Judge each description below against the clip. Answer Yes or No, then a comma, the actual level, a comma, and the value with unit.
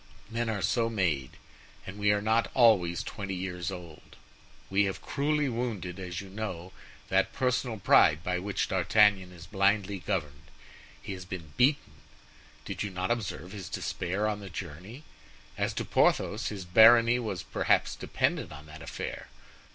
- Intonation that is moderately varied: Yes, average, 3.7 semitones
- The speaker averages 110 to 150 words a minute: No, average, 160 wpm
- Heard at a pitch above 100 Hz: No, very low, 95 Hz